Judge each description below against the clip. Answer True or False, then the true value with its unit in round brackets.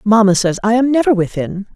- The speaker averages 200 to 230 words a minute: True (205 wpm)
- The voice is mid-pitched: False (215 Hz)